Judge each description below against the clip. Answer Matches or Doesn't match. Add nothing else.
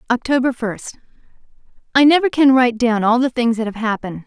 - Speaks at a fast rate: Doesn't match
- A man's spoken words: Doesn't match